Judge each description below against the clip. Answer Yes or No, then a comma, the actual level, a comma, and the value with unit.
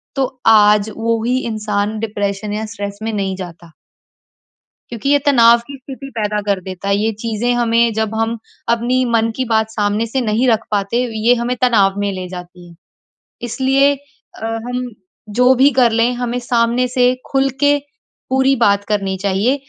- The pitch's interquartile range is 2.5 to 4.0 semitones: Yes, average, 3.3 semitones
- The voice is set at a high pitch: Yes, high, 225 Hz